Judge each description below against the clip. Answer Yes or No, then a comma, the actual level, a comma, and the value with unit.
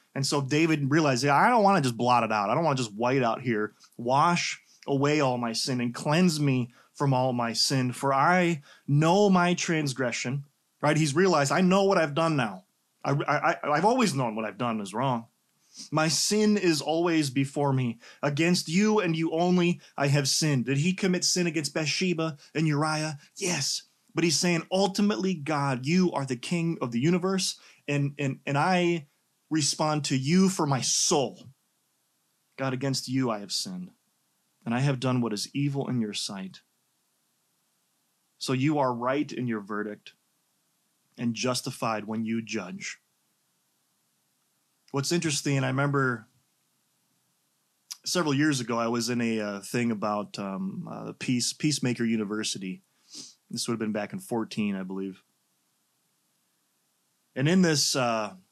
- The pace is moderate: Yes, average, 165 wpm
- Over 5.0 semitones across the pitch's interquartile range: Yes, wide, 5.6 semitones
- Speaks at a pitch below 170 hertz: Yes, medium, 140 Hz